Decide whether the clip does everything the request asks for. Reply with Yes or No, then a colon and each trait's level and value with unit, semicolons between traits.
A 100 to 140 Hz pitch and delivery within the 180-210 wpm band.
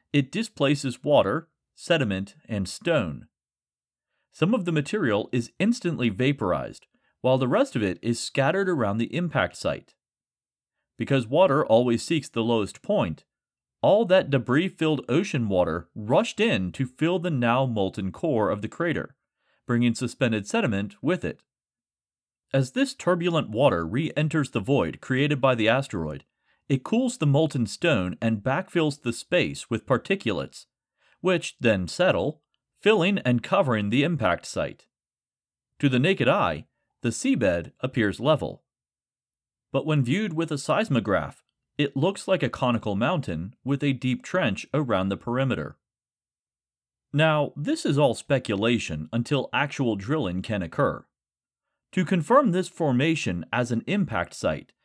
No: low, 135 Hz; average, 140 wpm